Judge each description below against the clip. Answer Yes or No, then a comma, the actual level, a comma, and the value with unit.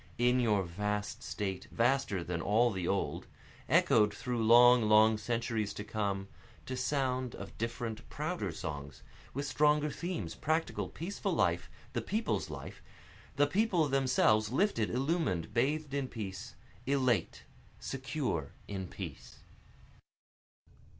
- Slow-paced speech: Yes, slow, 125 wpm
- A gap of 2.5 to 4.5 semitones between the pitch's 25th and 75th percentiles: No, average, 4.9 semitones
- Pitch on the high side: No, low, 120 Hz